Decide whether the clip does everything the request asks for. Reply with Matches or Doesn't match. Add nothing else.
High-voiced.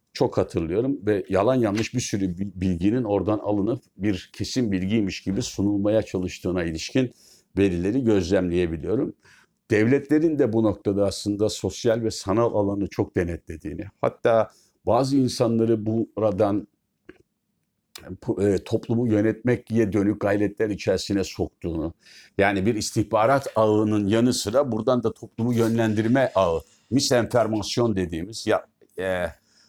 Doesn't match